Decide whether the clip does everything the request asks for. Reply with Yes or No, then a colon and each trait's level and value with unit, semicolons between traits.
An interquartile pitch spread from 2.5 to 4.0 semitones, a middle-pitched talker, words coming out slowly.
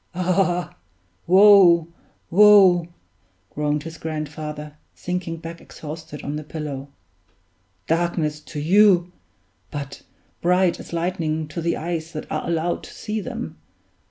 Yes: average, 2.8 semitones; medium, 170 Hz; slow, 120 wpm